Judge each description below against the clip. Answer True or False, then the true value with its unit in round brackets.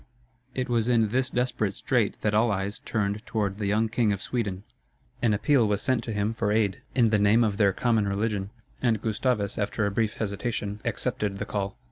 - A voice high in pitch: False (105 Hz)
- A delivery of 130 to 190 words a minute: False (200 wpm)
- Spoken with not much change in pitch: True (2.3 semitones)